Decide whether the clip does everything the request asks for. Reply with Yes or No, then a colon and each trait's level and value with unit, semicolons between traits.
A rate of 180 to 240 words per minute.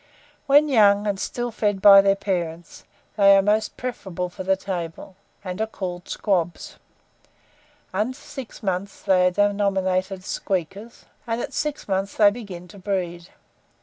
No: average, 150 wpm